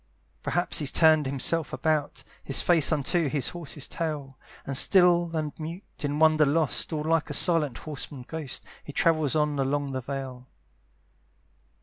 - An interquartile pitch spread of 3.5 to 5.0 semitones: No, average, 2.7 semitones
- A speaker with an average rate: Yes, average, 150 wpm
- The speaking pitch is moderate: Yes, medium, 150 Hz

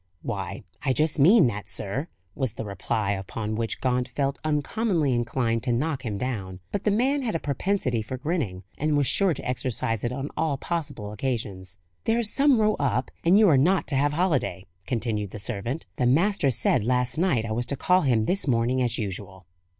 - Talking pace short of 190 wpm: No, average, 195 wpm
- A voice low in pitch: Yes, low, 130 Hz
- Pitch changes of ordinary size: No, wide, 6.1 semitones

